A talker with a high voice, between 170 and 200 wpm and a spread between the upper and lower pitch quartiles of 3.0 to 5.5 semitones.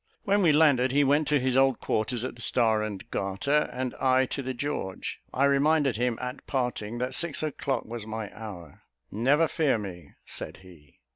No: low, 125 Hz; average, 190 wpm; average, 4.4 semitones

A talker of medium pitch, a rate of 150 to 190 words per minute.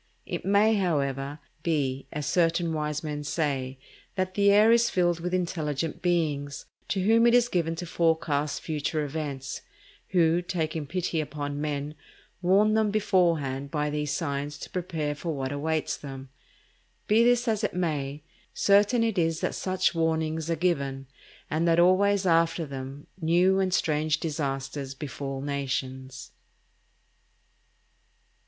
No: medium, 160 Hz; average, 140 wpm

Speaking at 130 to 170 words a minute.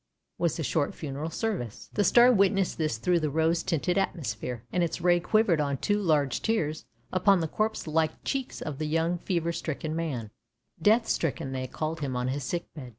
No: fast, 205 wpm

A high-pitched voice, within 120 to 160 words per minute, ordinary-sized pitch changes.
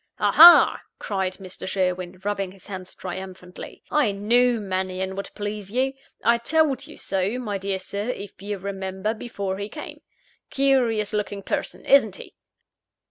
Yes: high, 200 Hz; average, 145 wpm; average, 3.3 semitones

